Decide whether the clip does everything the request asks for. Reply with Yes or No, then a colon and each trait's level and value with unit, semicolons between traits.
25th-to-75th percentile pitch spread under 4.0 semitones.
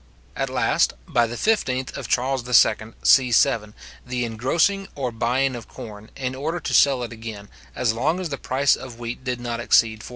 Yes: average, 2.7 semitones